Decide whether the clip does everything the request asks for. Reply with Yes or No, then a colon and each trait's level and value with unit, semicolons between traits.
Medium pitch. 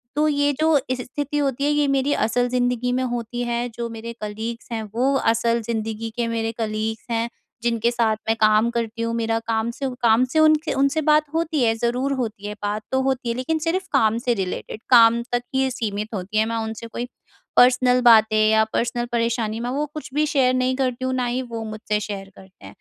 No: high, 235 Hz